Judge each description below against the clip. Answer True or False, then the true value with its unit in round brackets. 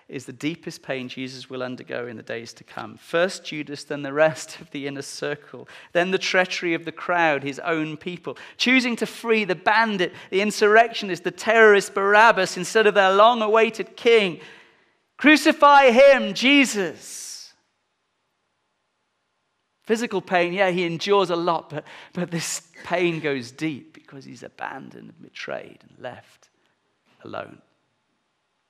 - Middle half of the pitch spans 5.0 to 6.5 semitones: True (5.6 semitones)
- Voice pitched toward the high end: False (180 Hz)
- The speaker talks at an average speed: True (145 wpm)